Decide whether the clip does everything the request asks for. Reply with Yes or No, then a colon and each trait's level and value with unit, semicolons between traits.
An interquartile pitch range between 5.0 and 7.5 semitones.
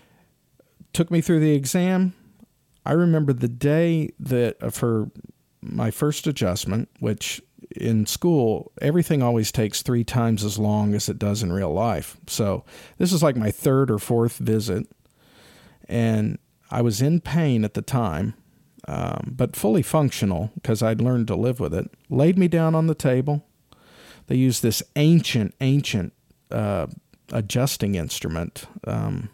Yes: wide, 5.6 semitones